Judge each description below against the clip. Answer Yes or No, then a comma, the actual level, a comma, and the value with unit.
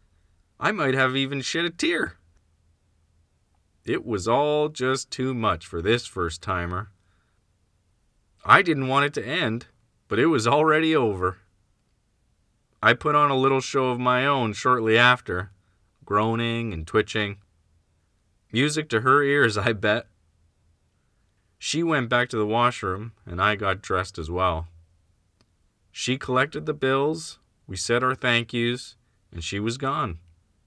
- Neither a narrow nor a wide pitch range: No, wide, 5.8 semitones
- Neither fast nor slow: Yes, average, 145 wpm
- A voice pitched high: No, low, 110 Hz